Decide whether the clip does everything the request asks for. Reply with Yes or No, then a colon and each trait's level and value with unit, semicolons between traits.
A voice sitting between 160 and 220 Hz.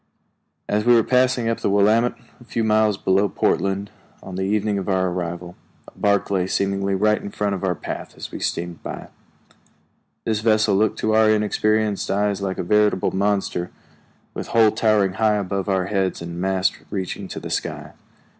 No: low, 100 Hz